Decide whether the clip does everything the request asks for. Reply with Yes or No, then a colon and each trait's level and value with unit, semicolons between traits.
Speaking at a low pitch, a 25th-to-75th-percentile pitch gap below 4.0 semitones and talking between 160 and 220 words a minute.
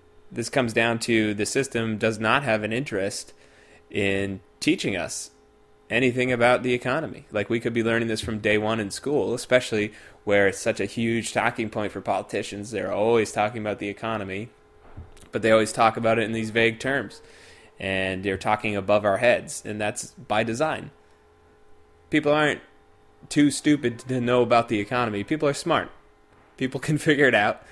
Yes: low, 110 Hz; average, 3.1 semitones; average, 180 wpm